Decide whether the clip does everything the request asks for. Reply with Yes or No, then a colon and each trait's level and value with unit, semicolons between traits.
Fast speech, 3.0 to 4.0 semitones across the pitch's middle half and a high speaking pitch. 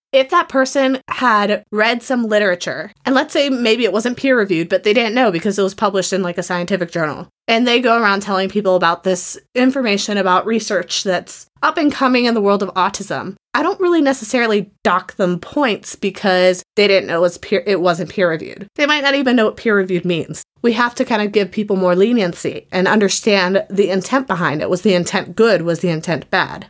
No: fast, 220 wpm; average, 4.7 semitones; high, 205 Hz